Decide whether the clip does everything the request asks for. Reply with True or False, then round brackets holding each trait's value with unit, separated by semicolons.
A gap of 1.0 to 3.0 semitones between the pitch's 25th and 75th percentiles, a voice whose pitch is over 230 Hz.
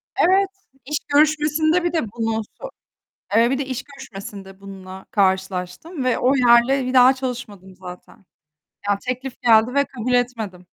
False (5.6 semitones; 245 Hz)